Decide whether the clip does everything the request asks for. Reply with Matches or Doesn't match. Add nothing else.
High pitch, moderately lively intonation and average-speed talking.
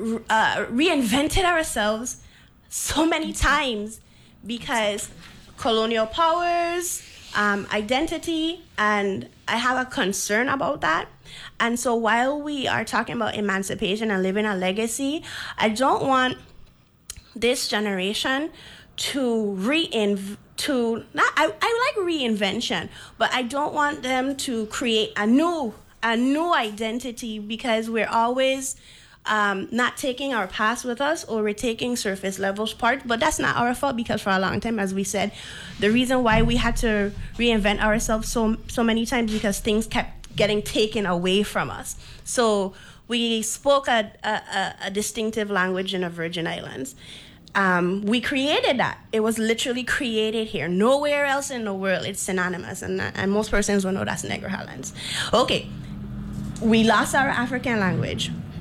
Matches